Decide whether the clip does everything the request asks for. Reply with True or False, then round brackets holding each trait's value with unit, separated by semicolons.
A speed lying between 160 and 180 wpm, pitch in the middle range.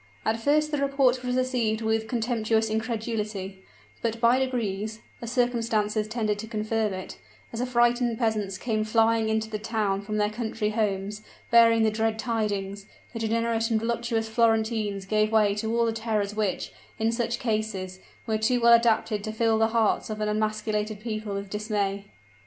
False (170 wpm; 220 Hz)